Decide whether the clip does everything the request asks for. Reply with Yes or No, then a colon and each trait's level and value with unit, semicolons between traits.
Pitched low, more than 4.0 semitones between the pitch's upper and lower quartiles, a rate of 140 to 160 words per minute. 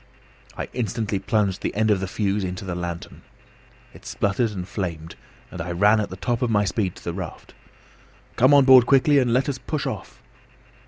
No: low, 105 Hz; average, 4.7 semitones; average, 200 wpm